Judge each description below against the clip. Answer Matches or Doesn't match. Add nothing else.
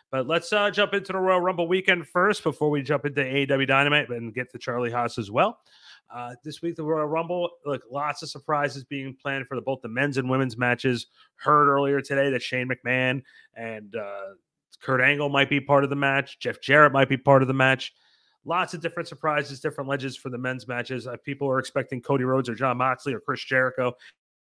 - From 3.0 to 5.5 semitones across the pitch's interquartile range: Doesn't match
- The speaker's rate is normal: Doesn't match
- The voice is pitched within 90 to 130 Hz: Doesn't match